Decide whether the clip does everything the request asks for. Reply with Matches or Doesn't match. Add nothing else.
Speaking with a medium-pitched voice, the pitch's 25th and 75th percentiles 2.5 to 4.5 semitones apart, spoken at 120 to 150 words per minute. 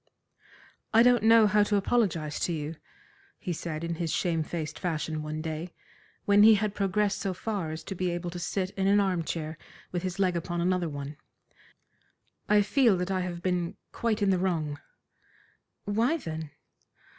Doesn't match